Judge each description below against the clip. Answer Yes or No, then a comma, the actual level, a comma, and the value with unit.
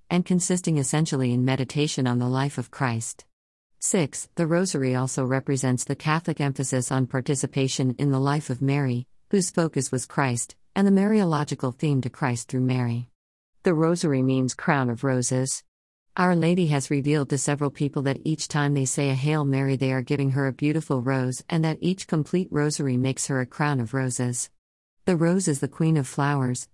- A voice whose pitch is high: No, medium, 140 Hz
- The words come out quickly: Yes, fast, 185 wpm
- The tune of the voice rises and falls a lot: No, average, 2.9 semitones